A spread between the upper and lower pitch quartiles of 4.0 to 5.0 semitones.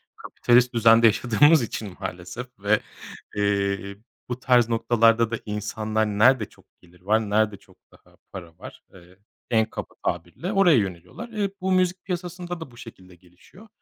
Yes: average, 4.5 semitones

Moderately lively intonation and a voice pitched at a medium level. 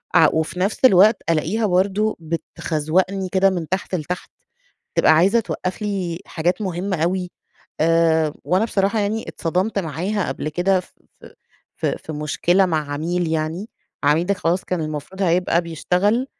Yes: average, 3.3 semitones; medium, 180 Hz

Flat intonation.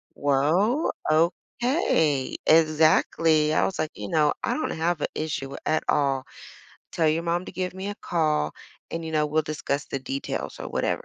Yes: narrow, 2.3 semitones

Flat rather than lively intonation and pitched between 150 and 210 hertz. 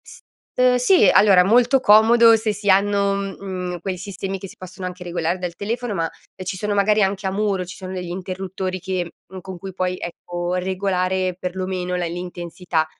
Yes: narrow, 1.9 semitones; high, 190 Hz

